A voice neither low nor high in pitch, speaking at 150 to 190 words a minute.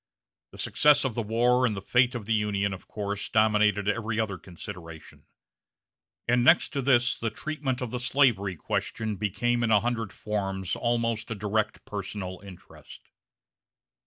No: low, 110 Hz; average, 155 wpm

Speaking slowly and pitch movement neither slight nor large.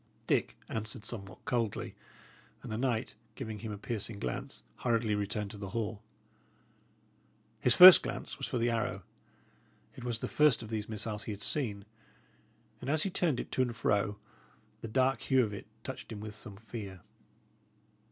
No: average, 170 wpm; average, 3.0 semitones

